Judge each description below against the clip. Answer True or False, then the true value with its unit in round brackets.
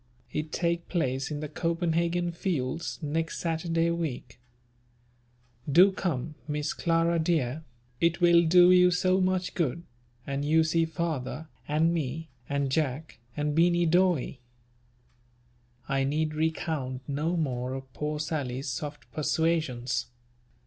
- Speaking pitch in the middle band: True (160 Hz)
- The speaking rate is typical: False (125 wpm)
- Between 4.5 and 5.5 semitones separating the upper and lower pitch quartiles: False (3.1 semitones)